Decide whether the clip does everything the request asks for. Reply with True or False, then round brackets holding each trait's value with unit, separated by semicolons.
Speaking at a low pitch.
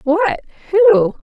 False (340 Hz)